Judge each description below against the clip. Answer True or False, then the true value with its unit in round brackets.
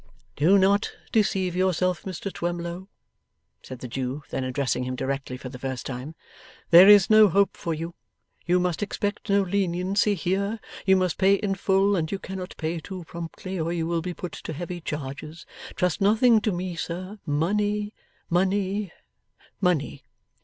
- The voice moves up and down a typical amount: True (3.6 semitones)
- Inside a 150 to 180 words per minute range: True (165 wpm)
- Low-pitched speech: False (180 Hz)